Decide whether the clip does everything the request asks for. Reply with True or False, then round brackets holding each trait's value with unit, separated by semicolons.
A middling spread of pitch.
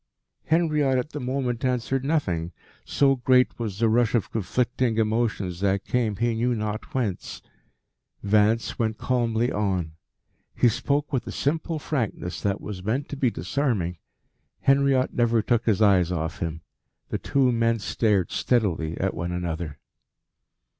True (4.7 semitones)